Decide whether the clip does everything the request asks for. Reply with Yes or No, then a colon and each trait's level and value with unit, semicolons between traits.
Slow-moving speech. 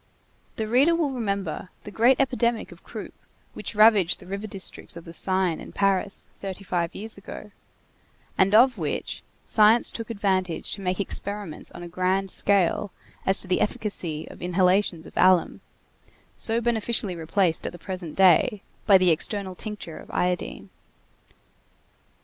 No: average, 155 wpm